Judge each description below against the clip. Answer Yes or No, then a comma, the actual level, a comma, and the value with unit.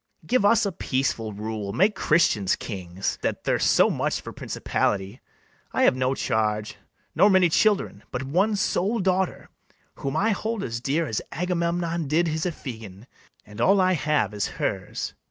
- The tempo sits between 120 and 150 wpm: No, average, 160 wpm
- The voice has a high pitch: No, medium, 155 Hz